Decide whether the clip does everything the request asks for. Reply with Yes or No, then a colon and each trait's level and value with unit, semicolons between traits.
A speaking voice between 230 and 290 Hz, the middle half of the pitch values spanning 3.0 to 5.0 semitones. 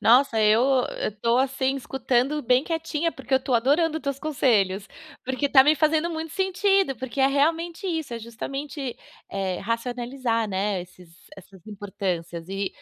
No: very high, 260 Hz; wide, 5.6 semitones